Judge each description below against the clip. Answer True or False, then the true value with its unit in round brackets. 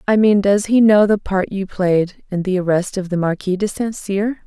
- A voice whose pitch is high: True (195 Hz)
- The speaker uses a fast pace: True (240 wpm)